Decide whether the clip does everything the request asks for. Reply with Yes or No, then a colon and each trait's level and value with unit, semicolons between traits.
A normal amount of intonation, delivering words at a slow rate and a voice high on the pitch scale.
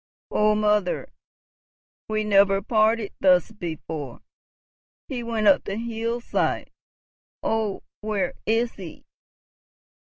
No: narrow, 2.3 semitones; slow, 95 wpm; high, 210 Hz